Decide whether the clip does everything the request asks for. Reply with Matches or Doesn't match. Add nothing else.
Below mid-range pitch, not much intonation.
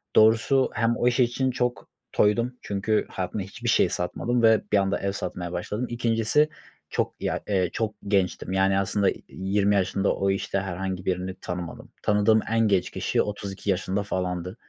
Doesn't match